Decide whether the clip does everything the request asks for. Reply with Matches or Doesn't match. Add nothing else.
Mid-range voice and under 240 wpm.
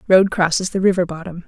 Matches